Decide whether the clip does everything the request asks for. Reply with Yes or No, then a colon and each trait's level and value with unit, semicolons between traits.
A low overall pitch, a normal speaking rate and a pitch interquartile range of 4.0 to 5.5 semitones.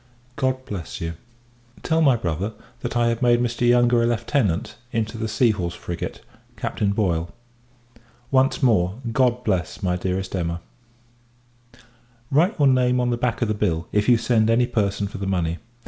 Yes: low, 110 Hz; average, 170 wpm; average, 4.5 semitones